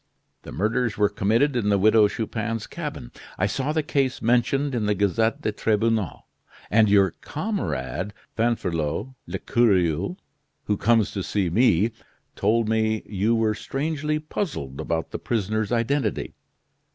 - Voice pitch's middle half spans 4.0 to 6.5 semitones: No, average, 3.2 semitones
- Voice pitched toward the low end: Yes, low, 110 Hz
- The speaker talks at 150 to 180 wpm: No, average, 140 wpm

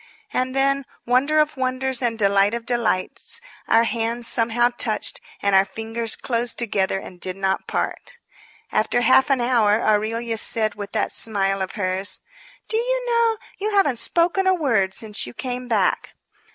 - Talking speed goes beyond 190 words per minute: No, average, 165 wpm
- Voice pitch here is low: No, high, 235 Hz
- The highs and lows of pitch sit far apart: No, average, 4.1 semitones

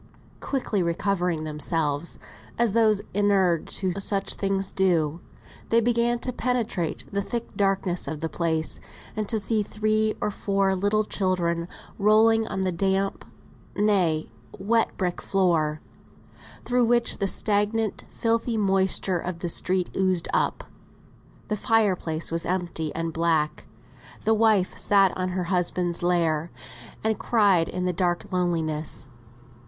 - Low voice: No, high, 190 Hz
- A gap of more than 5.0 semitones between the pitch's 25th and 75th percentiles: No, average, 3.8 semitones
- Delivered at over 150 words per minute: No, slow, 135 wpm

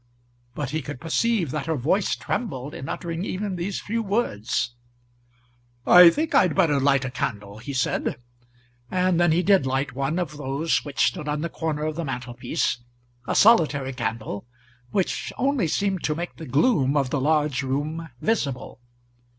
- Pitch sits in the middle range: Yes, medium, 150 Hz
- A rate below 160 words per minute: No, average, 165 wpm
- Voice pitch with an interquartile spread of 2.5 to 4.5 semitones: No, average, 5.0 semitones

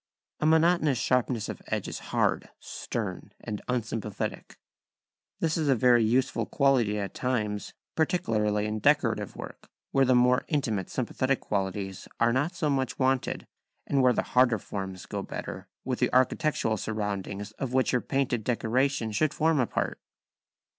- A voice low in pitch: Yes, low, 125 Hz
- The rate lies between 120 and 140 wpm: No, average, 150 wpm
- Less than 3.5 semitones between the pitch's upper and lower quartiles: No, average, 4.2 semitones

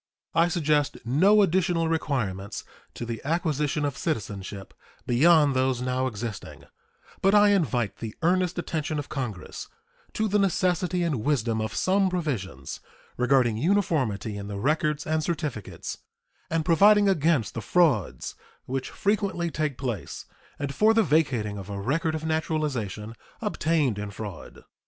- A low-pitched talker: No, medium, 150 Hz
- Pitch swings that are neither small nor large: No, wide, 6.9 semitones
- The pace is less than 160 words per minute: Yes, average, 140 wpm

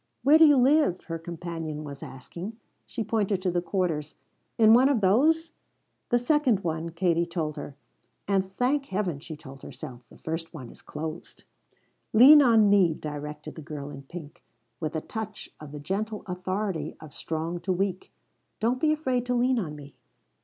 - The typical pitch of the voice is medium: Yes, medium, 180 Hz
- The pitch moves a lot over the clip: Yes, wide, 6.4 semitones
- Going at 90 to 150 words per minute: No, average, 175 wpm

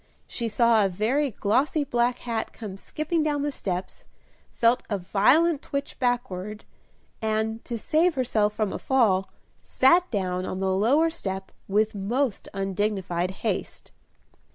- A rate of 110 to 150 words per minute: Yes, average, 140 wpm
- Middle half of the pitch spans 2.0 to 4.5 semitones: No, average, 5.3 semitones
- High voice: Yes, high, 220 Hz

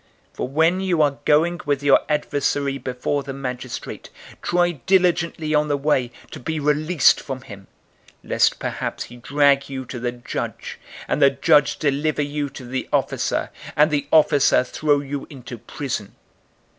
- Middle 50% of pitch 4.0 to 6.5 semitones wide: No, narrow, 2.4 semitones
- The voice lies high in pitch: No, medium, 145 Hz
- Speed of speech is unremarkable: Yes, average, 160 wpm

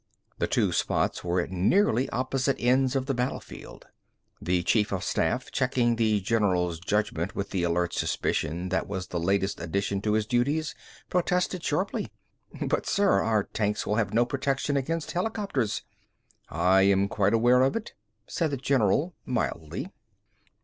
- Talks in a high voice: No, low, 110 Hz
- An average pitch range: No, wide, 5.9 semitones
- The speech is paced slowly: No, average, 155 wpm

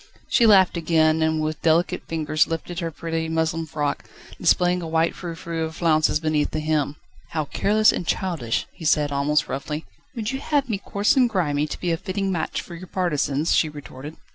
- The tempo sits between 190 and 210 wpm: Yes, average, 195 wpm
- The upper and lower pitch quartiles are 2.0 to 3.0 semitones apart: Yes, narrow, 2.6 semitones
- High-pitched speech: No, medium, 160 Hz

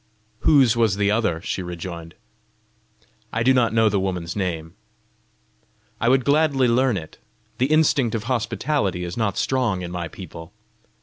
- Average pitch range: No, wide, 6.2 semitones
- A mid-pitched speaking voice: No, low, 105 Hz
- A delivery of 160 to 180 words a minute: No, average, 150 wpm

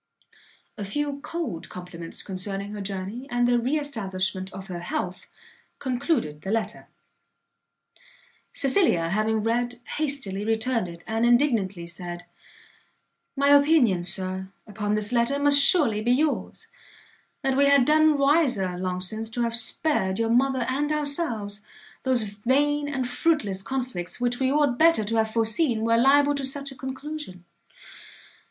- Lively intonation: Yes, wide, 6.2 semitones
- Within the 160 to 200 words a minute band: No, average, 145 wpm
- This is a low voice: No, high, 235 Hz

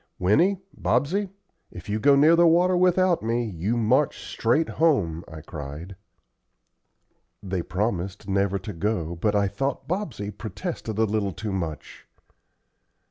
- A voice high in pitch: No, low, 105 Hz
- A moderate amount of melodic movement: No, wide, 7.5 semitones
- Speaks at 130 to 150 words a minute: Yes, slow, 135 wpm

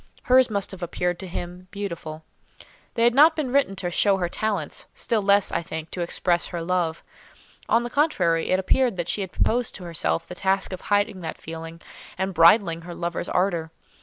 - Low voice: No, medium, 185 Hz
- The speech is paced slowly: No, average, 195 wpm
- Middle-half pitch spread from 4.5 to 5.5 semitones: No, average, 3.1 semitones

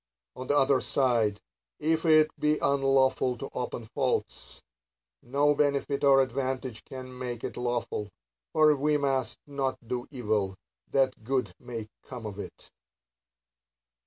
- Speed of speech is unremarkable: No, slow, 130 wpm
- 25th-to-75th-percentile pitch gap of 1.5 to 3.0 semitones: Yes, narrow, 2.5 semitones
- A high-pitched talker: No, low, 130 Hz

